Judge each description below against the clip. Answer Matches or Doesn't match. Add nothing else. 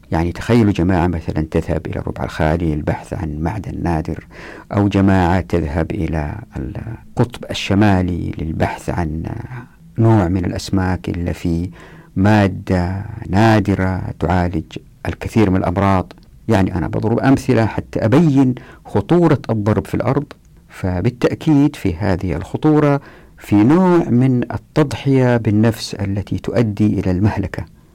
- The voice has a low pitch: Matches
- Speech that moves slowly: Doesn't match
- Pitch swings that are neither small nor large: Matches